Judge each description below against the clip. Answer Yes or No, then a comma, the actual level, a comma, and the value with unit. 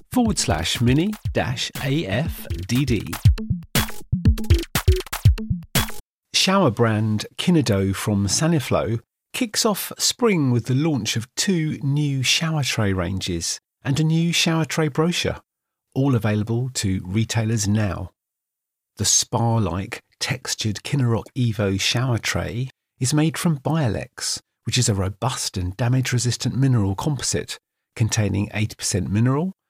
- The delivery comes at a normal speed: No, slow, 115 wpm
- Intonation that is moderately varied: No, wide, 5.9 semitones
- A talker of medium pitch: No, low, 120 Hz